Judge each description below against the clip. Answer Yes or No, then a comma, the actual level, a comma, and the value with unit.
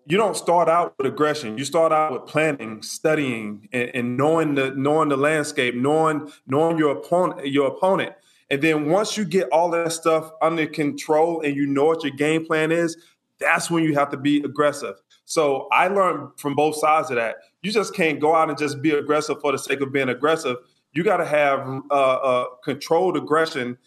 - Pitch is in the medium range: Yes, medium, 150 Hz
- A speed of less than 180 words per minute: No, fast, 205 wpm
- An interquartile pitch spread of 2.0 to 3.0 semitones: Yes, narrow, 2.5 semitones